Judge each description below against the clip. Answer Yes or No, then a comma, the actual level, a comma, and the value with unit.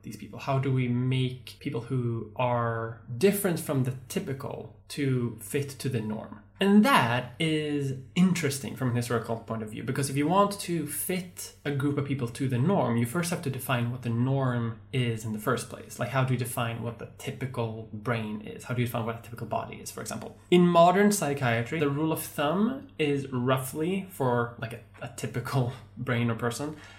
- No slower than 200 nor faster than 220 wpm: Yes, fast, 205 wpm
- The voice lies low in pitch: Yes, low, 125 Hz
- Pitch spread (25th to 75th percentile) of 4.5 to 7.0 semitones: No, average, 3.7 semitones